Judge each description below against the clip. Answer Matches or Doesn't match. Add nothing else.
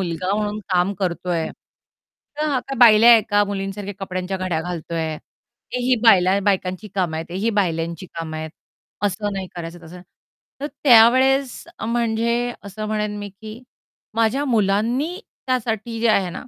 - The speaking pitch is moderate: Doesn't match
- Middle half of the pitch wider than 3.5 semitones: Matches